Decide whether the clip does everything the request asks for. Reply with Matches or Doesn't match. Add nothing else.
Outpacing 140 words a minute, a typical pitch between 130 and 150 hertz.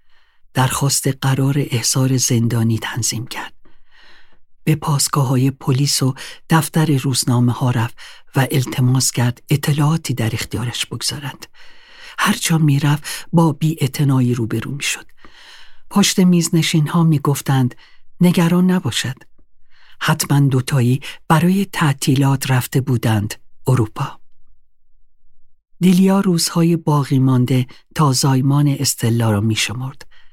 Doesn't match